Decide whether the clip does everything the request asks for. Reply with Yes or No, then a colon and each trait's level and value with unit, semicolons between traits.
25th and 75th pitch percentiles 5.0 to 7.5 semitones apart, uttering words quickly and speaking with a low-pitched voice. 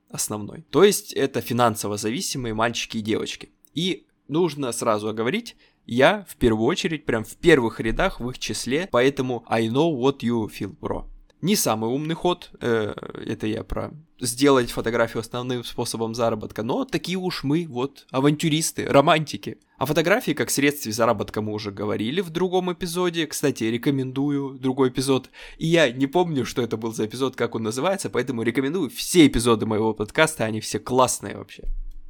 Yes: average, 5.3 semitones; fast, 165 wpm; low, 125 Hz